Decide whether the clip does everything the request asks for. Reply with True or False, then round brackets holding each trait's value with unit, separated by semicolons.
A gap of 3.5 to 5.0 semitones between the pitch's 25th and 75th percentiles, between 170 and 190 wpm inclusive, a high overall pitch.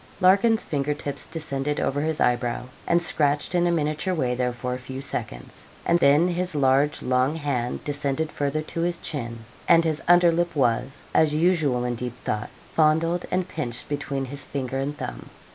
False (4.0 semitones; 180 wpm; 145 Hz)